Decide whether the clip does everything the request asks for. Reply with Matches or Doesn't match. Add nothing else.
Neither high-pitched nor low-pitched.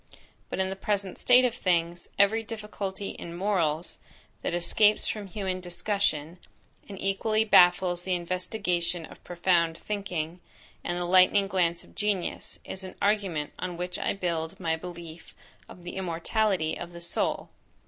Matches